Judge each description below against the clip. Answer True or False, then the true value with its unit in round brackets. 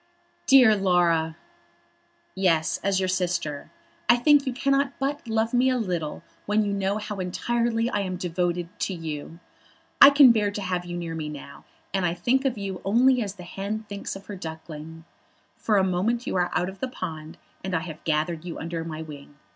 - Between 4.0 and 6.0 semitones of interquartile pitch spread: True (5.0 semitones)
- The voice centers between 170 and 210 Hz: True (190 Hz)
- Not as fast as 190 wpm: False (195 wpm)